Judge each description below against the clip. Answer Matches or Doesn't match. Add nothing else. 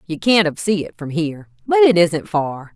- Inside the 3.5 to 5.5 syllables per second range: Matches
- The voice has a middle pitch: Matches